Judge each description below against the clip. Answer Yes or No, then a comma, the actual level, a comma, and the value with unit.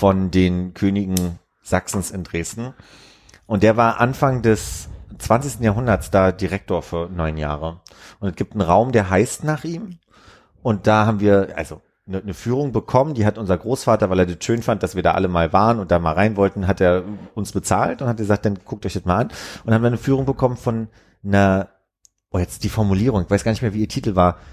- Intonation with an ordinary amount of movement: Yes, average, 3.7 semitones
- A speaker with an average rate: No, fast, 220 wpm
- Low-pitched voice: Yes, low, 100 Hz